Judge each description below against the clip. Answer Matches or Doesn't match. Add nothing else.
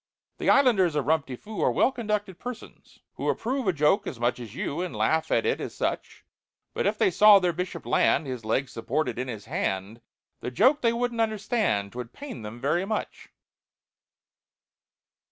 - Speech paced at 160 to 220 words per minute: Matches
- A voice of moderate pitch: Matches